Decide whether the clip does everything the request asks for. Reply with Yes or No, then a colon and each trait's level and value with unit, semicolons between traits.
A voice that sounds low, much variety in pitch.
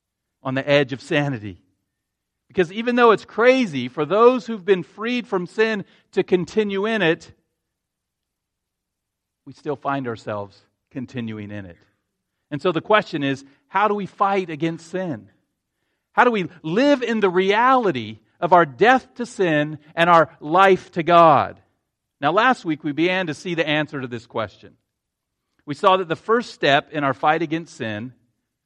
No: medium, 160 Hz; wide, 6.6 semitones